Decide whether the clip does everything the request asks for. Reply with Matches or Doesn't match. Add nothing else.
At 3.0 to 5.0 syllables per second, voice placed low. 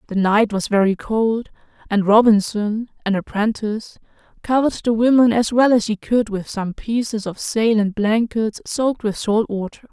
Doesn't match